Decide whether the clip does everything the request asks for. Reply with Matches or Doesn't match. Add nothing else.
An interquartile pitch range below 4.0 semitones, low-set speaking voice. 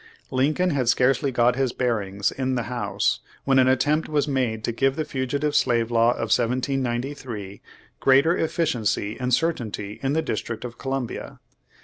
Matches